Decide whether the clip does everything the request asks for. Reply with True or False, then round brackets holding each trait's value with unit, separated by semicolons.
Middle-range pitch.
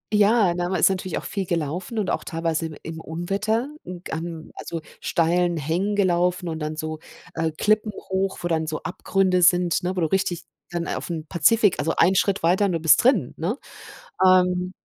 True (180 Hz)